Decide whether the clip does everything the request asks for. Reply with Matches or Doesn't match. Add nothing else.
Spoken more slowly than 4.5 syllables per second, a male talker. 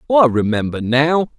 Doesn't match